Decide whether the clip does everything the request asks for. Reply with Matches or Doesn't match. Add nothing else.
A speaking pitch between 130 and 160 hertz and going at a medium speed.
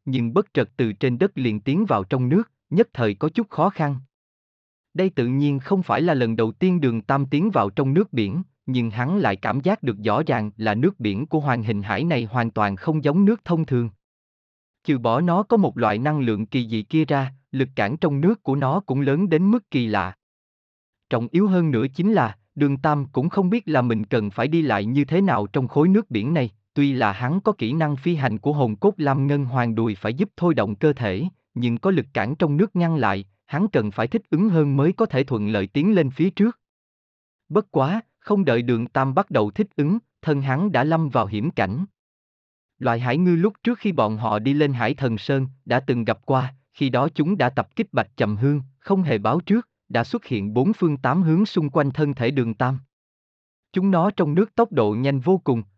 Matches